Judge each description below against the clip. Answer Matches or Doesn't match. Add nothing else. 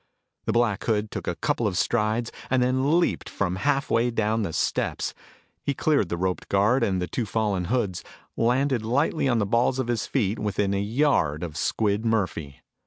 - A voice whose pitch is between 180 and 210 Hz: Doesn't match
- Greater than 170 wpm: Matches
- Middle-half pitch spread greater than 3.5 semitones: Matches